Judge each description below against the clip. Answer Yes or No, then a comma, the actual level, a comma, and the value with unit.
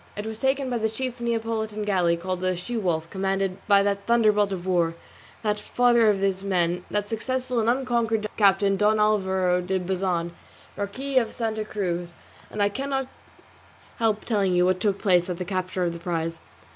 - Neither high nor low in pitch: No, high, 200 Hz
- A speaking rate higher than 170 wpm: Yes, average, 185 wpm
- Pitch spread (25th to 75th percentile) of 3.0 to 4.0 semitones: Yes, average, 3.4 semitones